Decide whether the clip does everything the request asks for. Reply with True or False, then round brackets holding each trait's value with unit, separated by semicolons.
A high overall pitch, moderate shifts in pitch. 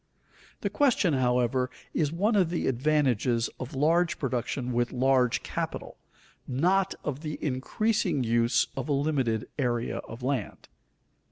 False (135 Hz; 4.2 semitones)